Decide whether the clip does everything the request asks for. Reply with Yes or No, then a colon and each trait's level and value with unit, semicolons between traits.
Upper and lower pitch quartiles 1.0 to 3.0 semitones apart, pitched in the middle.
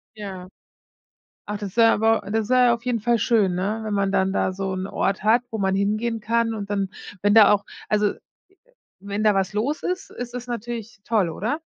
No: average, 2.7 semitones; high, 210 Hz